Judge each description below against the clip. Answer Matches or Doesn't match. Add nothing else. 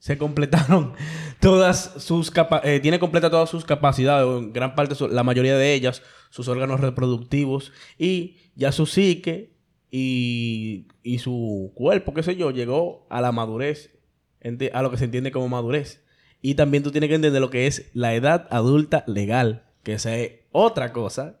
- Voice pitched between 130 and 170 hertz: Matches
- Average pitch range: Matches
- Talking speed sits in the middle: Matches